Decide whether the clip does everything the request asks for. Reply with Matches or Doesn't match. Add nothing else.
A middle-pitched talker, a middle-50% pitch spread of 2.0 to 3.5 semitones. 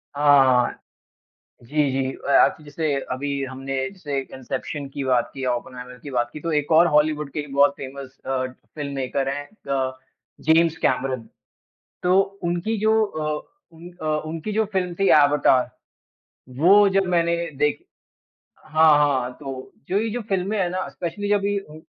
Doesn't match